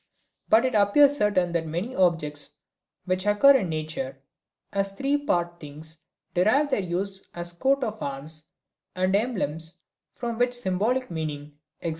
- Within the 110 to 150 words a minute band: Yes, average, 145 wpm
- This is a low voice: No, medium, 185 Hz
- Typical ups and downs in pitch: No, wide, 6.1 semitones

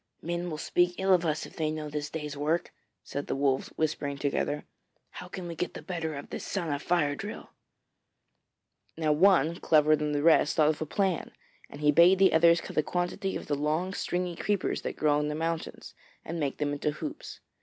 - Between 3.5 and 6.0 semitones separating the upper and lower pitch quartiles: No, average, 3.0 semitones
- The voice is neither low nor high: Yes, medium, 155 Hz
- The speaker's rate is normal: No, fast, 215 wpm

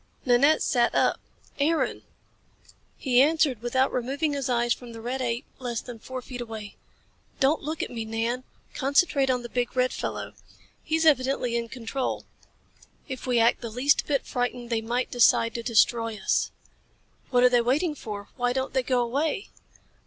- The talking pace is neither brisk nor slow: Yes, average, 170 wpm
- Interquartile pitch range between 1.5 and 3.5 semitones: Yes, narrow, 2.4 semitones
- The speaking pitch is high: Yes, very high, 250 Hz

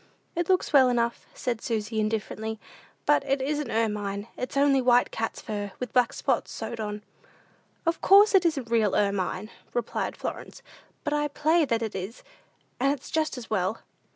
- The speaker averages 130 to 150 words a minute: No, average, 170 wpm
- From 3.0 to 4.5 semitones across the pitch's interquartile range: No, average, 4.9 semitones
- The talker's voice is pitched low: No, high, 235 Hz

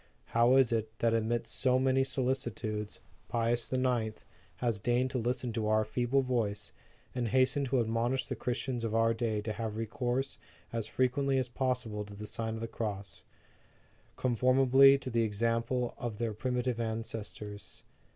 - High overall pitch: No, low, 120 Hz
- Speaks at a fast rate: No, average, 160 wpm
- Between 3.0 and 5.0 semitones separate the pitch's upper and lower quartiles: No, narrow, 2.4 semitones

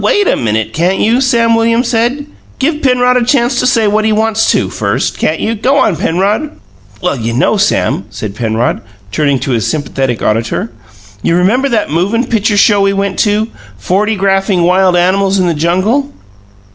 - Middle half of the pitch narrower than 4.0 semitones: No, wide, 5.5 semitones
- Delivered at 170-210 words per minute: Yes, average, 185 wpm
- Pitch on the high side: Yes, high, 200 Hz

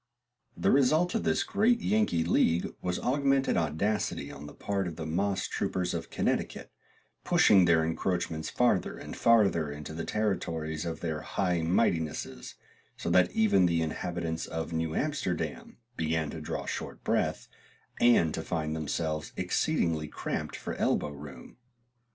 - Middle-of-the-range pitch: No, very low, 85 Hz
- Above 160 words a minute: No, average, 145 wpm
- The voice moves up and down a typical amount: Yes, average, 4.2 semitones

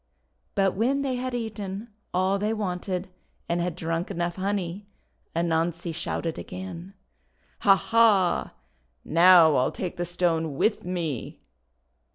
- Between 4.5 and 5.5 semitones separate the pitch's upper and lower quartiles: No, average, 3.0 semitones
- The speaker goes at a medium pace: No, slow, 130 wpm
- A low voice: No, medium, 180 Hz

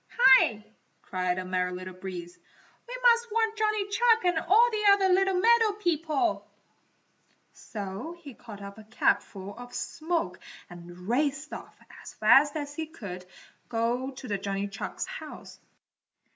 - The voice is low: No, very high, 270 Hz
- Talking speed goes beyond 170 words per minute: No, average, 145 wpm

